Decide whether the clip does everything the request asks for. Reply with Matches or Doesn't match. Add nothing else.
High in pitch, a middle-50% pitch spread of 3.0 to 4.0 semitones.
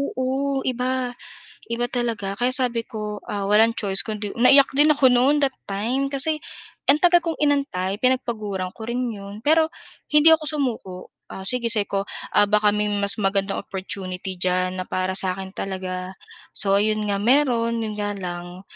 Doesn't match